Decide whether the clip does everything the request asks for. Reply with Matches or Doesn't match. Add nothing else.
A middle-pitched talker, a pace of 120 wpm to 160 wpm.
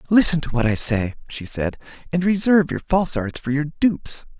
Doesn't match